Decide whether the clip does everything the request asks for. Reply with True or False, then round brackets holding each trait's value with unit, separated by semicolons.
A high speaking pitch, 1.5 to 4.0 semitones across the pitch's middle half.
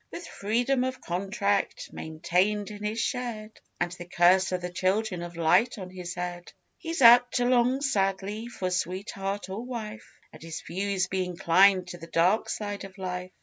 True (195 Hz; 3.5 semitones)